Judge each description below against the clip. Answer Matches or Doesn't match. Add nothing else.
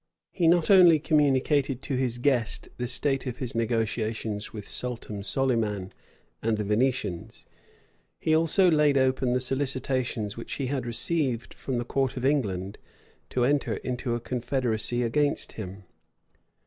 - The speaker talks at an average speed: Matches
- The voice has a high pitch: Doesn't match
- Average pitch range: Matches